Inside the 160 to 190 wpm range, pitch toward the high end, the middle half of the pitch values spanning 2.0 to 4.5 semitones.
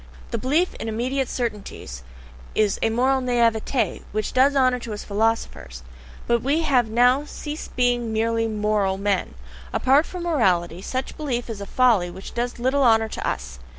Yes: average, 170 wpm; high, 235 Hz; average, 3.5 semitones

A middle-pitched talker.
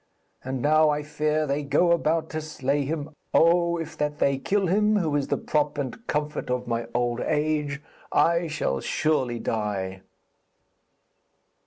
Yes: medium, 150 Hz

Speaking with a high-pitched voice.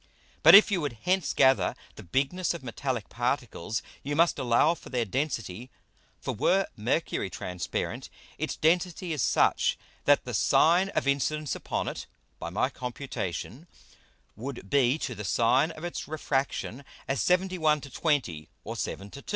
No: medium, 140 Hz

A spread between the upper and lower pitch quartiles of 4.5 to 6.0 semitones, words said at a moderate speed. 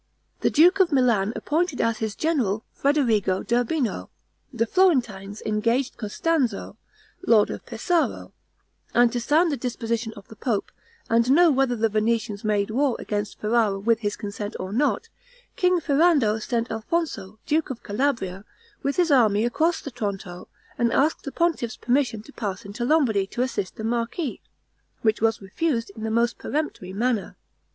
Yes: average, 5.0 semitones; average, 160 wpm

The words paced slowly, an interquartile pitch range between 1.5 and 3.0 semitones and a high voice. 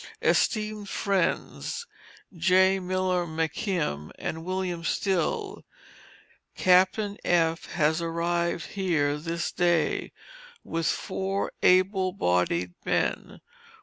No: slow, 85 wpm; narrow, 2.5 semitones; medium, 180 Hz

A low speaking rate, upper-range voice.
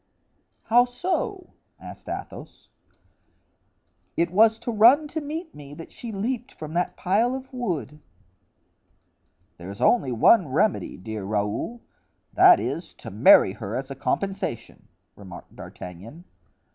Yes: slow, 120 wpm; high, 195 Hz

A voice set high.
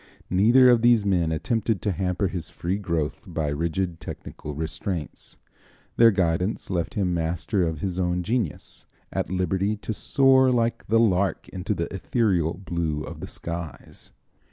No: very low, 95 Hz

